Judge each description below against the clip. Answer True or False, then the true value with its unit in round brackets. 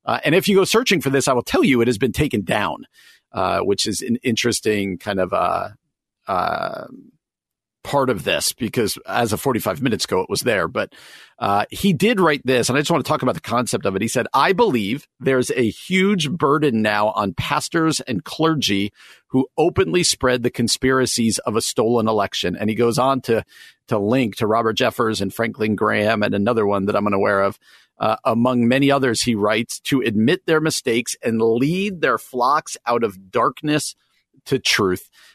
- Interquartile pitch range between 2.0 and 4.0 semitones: False (4.7 semitones)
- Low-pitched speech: True (120 Hz)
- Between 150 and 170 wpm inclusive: False (200 wpm)